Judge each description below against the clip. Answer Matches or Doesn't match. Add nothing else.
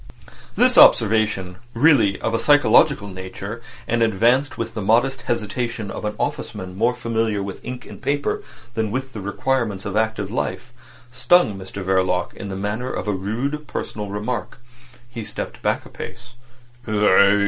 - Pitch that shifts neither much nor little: Matches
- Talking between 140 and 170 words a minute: Matches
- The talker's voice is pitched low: Matches